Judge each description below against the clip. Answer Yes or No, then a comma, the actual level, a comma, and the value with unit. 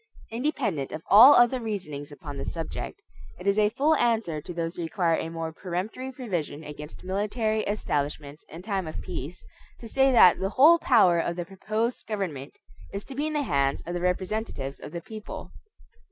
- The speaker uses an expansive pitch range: Yes, wide, 5.7 semitones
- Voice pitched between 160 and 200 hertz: Yes, medium, 185 Hz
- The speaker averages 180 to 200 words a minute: Yes, average, 185 wpm